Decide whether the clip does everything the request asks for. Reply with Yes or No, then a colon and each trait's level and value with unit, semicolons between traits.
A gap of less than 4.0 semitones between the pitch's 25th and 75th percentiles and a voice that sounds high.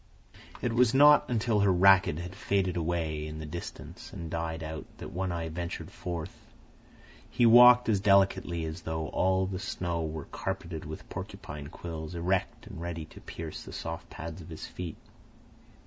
No: average, 3.3 semitones; very low, 85 Hz